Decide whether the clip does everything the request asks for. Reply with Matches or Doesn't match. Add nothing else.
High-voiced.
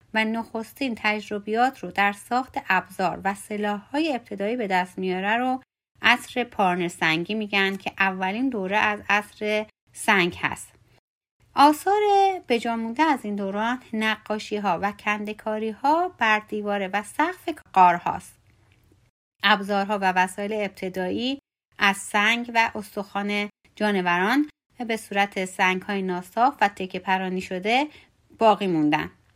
Matches